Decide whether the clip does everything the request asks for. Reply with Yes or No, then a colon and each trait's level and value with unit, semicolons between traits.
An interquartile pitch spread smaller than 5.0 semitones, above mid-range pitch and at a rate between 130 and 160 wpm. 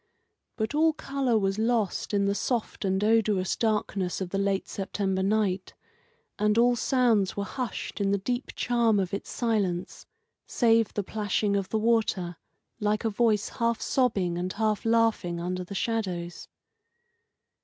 Yes: average, 2.9 semitones; high, 210 Hz; average, 155 wpm